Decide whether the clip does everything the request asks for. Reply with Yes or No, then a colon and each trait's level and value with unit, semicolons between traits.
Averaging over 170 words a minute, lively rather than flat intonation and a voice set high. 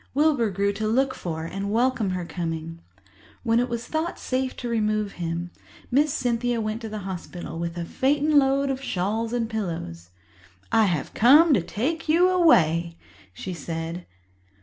No: average, 165 wpm; wide, 7.1 semitones; high, 220 Hz